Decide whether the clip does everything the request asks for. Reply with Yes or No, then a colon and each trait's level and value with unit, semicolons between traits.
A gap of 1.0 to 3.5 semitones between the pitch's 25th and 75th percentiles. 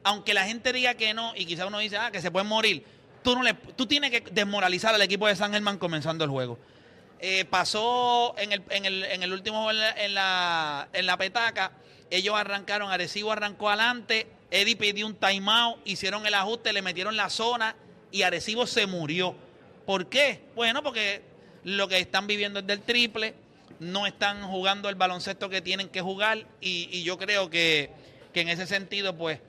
Yes: average, 2.9 semitones